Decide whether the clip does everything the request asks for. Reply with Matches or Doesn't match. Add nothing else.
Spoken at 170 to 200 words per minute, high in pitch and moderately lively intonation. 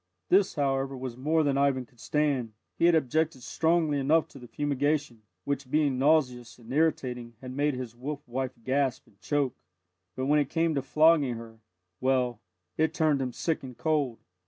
Doesn't match